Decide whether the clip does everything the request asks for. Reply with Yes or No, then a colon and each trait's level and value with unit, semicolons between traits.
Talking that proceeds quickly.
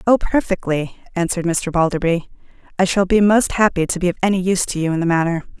Yes: fast, 215 wpm